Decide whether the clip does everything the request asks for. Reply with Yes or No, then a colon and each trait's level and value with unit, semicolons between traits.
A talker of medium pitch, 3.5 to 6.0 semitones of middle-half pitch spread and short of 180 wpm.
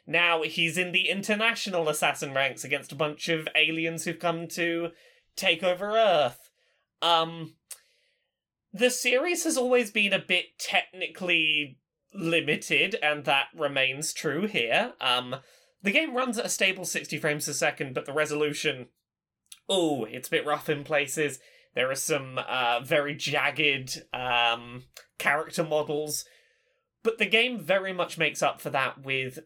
Yes: medium, 160 Hz; average, 3.9 semitones; average, 150 wpm